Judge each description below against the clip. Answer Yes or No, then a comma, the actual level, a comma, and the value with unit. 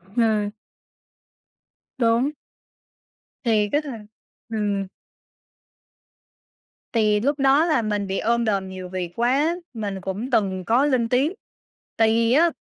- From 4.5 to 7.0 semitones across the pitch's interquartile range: No, average, 4.0 semitones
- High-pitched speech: Yes, high, 225 Hz